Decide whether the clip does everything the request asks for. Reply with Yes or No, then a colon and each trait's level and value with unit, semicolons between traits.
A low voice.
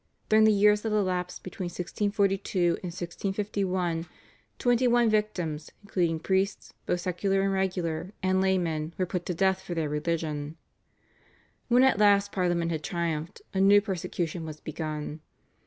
No: medium, 185 Hz